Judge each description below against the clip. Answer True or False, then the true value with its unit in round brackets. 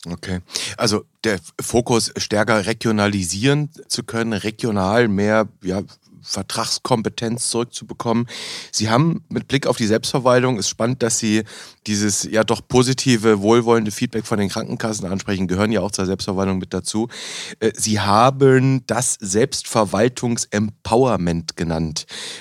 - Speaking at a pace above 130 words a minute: False (125 wpm)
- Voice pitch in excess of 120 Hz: False (110 Hz)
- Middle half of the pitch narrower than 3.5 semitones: True (2.8 semitones)